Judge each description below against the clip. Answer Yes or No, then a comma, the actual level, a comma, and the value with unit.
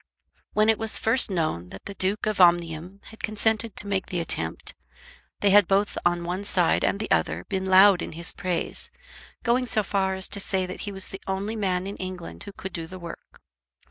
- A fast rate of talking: Yes, fast, 210 wpm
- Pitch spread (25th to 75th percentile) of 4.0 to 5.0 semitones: No, average, 2.8 semitones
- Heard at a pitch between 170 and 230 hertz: Yes, high, 190 Hz